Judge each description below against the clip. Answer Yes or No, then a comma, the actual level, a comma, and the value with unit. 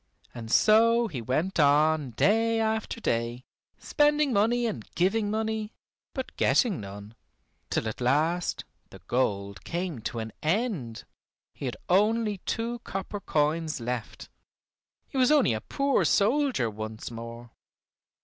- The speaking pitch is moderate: Yes, medium, 175 Hz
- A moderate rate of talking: No, slow, 130 wpm